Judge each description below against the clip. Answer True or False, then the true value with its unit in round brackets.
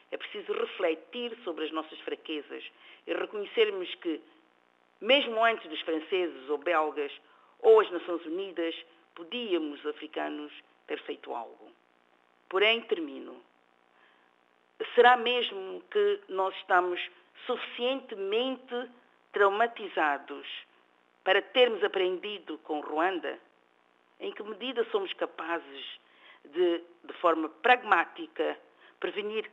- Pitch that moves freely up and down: True (8.8 semitones)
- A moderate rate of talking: False (100 wpm)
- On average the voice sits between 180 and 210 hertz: True (185 Hz)